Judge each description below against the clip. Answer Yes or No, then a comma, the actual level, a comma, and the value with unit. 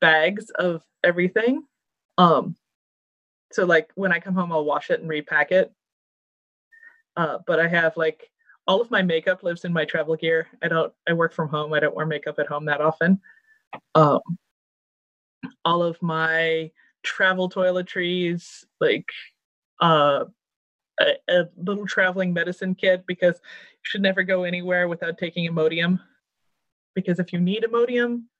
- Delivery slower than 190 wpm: Yes, average, 150 wpm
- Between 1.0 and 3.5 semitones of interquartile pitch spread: Yes, average, 2.8 semitones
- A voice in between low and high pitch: Yes, medium, 180 Hz